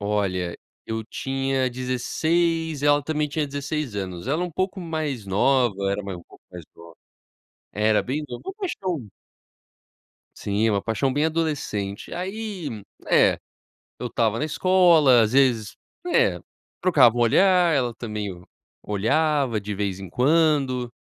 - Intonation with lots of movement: Yes, wide, 6.9 semitones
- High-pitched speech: No, low, 130 Hz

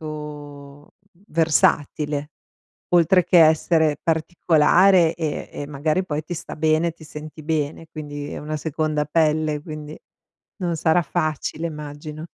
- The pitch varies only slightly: Yes, narrow, 1.6 semitones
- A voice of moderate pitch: Yes, medium, 155 Hz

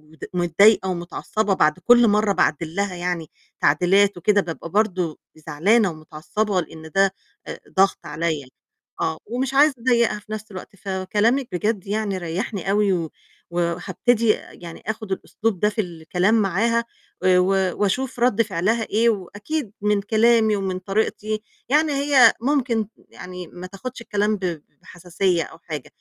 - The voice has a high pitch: Yes, high, 200 Hz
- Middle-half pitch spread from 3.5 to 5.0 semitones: Yes, average, 3.8 semitones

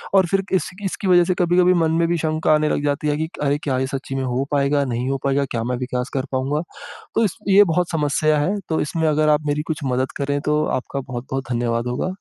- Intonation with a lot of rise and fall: No, average, 3.4 semitones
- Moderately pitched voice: Yes, medium, 145 Hz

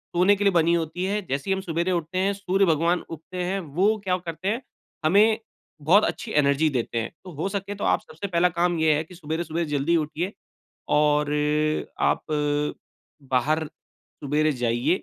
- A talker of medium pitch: Yes, medium, 170 Hz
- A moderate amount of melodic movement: Yes, average, 3.8 semitones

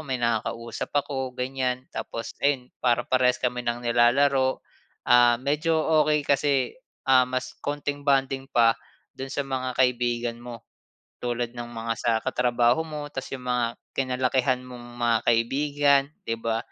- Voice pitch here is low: Yes, low, 125 Hz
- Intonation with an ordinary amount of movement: No, narrow, 2.1 semitones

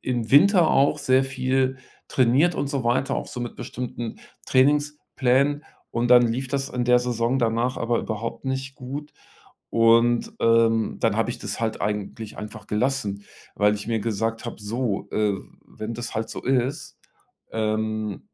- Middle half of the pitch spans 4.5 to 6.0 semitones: No, average, 2.9 semitones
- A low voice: Yes, low, 120 Hz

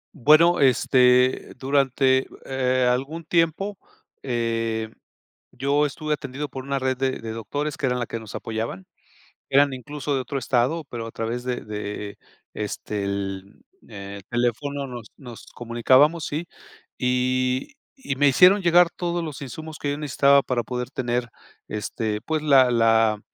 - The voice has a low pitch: Yes, low, 130 Hz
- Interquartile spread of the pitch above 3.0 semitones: Yes, average, 3.7 semitones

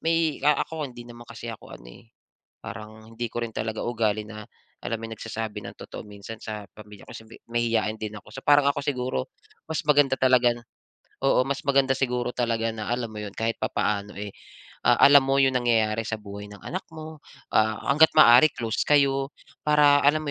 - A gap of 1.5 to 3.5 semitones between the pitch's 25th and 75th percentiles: No, average, 4.1 semitones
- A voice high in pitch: No, low, 120 Hz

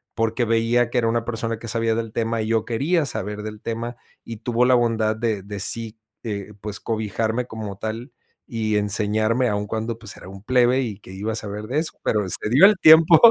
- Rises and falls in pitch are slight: Yes, narrow, 1.9 semitones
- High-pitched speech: No, low, 115 Hz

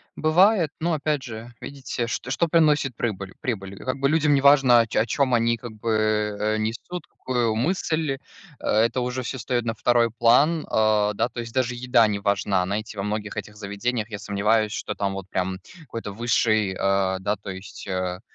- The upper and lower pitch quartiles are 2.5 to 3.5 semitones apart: No, average, 4.1 semitones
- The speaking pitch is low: Yes, low, 115 Hz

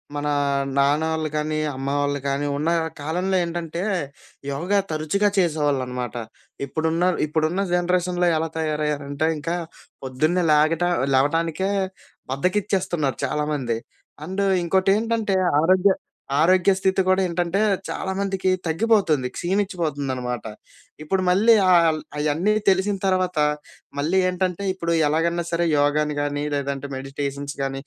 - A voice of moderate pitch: Yes, medium, 165 Hz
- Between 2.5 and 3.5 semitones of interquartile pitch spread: No, average, 4.3 semitones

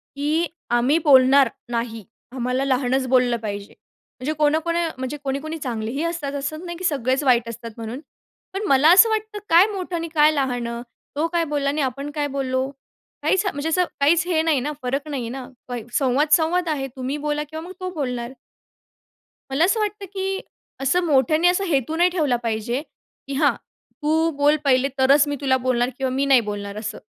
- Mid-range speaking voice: No, very high, 280 Hz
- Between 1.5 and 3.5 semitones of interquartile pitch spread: No, average, 4.1 semitones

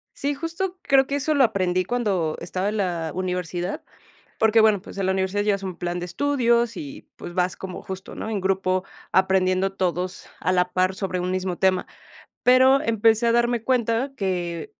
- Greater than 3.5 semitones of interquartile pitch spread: Yes, average, 4.3 semitones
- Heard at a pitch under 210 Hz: Yes, high, 190 Hz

